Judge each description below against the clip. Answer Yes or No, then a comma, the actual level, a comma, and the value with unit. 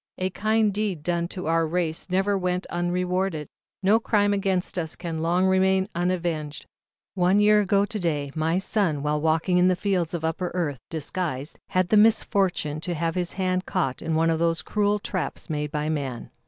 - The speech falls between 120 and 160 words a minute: No, average, 190 wpm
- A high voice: No, medium, 180 Hz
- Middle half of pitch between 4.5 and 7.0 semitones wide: No, average, 3.0 semitones